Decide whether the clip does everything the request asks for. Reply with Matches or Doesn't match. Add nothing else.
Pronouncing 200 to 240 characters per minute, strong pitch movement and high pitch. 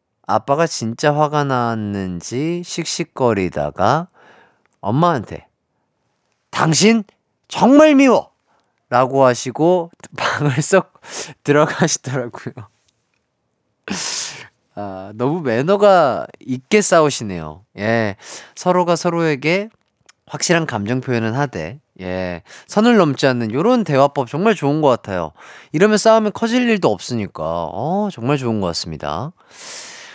Doesn't match